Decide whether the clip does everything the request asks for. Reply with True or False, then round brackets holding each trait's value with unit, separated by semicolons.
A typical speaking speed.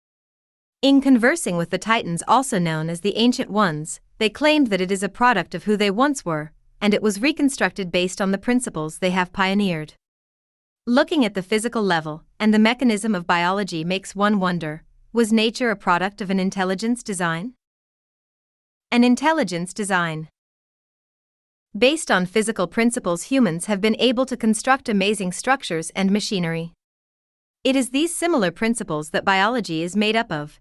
True (165 wpm)